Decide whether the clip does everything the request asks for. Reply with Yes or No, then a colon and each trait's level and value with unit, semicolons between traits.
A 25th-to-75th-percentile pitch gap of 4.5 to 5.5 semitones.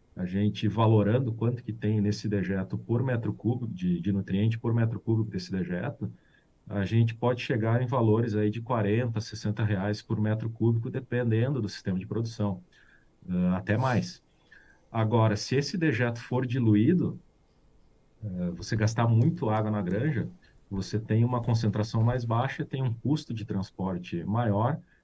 No: narrow, 2.5 semitones